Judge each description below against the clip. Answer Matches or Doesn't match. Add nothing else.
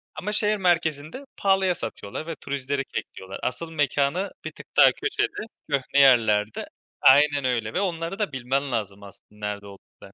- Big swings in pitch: Matches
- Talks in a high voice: Doesn't match